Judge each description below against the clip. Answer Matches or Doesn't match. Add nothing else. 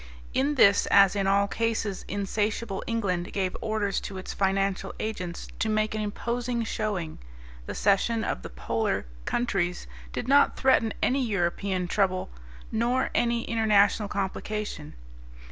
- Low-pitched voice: Doesn't match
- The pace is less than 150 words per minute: Matches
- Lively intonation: Doesn't match